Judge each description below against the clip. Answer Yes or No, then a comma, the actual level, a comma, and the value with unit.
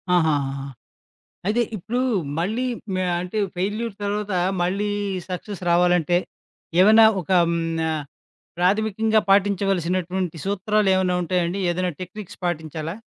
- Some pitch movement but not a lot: Yes, average, 3.1 semitones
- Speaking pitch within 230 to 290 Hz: No, medium, 185 Hz